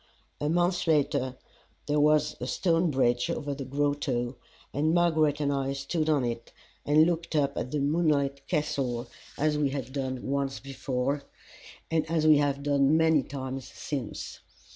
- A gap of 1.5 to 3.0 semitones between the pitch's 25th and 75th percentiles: Yes, narrow, 2.4 semitones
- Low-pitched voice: No, medium, 145 Hz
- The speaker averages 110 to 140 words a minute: No, average, 160 wpm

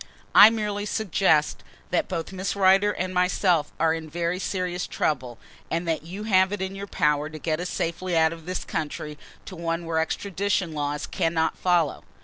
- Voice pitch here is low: No, medium, 175 Hz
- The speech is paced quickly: No, average, 180 wpm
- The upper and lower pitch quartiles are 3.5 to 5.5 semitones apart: No, average, 2.9 semitones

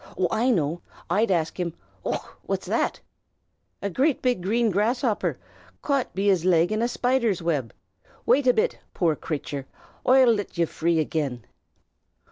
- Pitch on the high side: Yes, high, 195 Hz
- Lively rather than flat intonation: Yes, wide, 6.5 semitones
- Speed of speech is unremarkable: Yes, average, 150 wpm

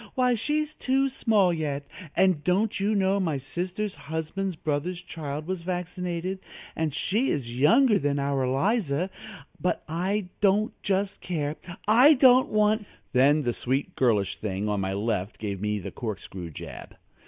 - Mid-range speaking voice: Yes, medium, 175 Hz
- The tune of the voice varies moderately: No, wide, 6.7 semitones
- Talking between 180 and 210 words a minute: No, average, 155 wpm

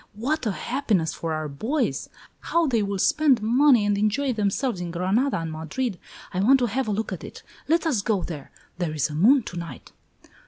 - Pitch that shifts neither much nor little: No, wide, 7.0 semitones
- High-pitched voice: Yes, high, 215 Hz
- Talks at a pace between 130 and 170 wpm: No, fast, 205 wpm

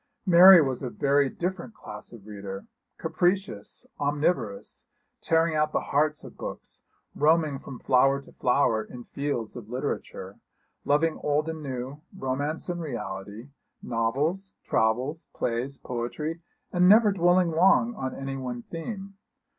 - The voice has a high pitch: No, medium, 145 Hz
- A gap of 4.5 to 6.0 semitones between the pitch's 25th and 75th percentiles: Yes, average, 5.1 semitones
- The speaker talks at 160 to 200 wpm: No, average, 140 wpm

